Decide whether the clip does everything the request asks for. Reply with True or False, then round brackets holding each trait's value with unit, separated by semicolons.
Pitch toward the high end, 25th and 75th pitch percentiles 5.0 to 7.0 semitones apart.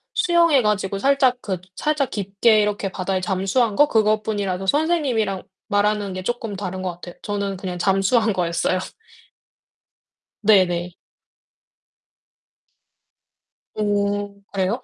False (205 Hz; 3.0 semitones)